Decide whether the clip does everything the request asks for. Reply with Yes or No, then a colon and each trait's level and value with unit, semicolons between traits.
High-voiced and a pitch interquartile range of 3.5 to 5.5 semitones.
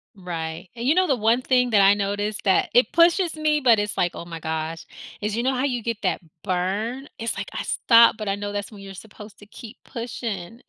Yes: high, 215 Hz; average, 3.9 semitones